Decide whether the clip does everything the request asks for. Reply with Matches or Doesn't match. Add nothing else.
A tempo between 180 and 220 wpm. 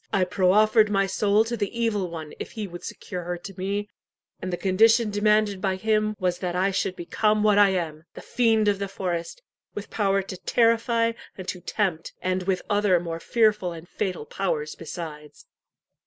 Matches